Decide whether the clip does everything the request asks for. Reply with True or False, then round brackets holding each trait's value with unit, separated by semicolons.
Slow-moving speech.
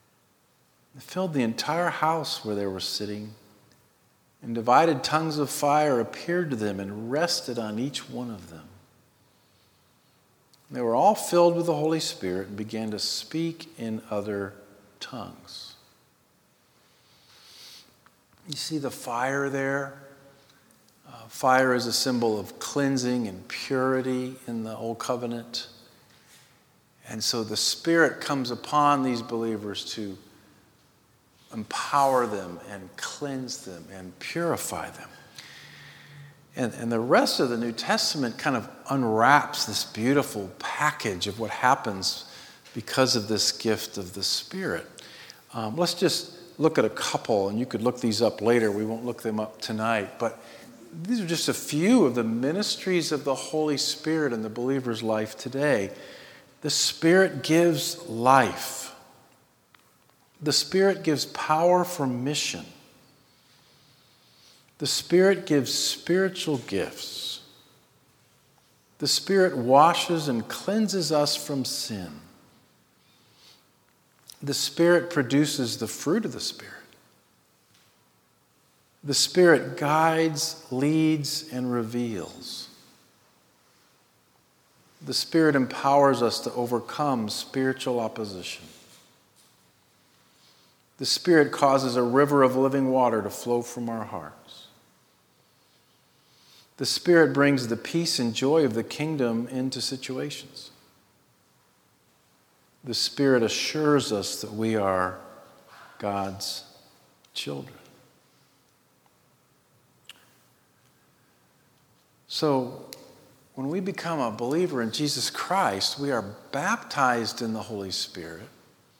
True (115 wpm)